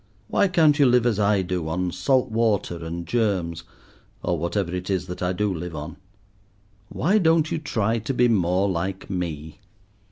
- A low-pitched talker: Yes, very low, 95 Hz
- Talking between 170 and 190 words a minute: Yes, average, 180 wpm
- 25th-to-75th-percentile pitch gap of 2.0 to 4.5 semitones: No, average, 5.2 semitones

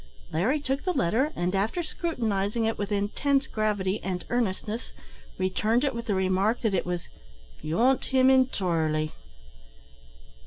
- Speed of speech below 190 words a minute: Yes, average, 140 wpm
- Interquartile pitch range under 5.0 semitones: No, wide, 5.5 semitones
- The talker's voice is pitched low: No, high, 215 Hz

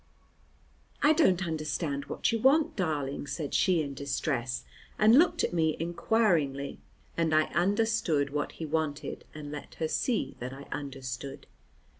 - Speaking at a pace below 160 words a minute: Yes, average, 145 wpm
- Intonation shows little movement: No, average, 4.8 semitones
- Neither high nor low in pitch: Yes, medium, 155 Hz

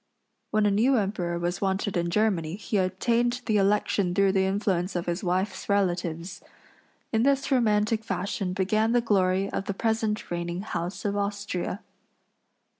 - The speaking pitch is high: Yes, high, 200 Hz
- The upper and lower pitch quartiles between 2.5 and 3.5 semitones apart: Yes, average, 2.9 semitones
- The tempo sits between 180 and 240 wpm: No, average, 155 wpm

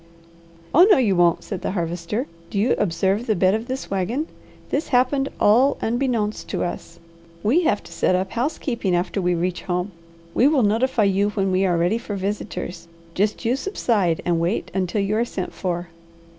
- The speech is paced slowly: No, average, 185 wpm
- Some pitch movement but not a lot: Yes, average, 4.9 semitones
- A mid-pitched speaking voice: No, high, 205 Hz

